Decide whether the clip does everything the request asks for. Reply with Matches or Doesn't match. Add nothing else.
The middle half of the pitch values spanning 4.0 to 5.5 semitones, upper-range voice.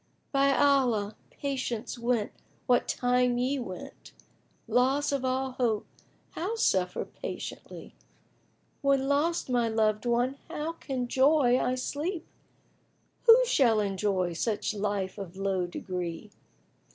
Matches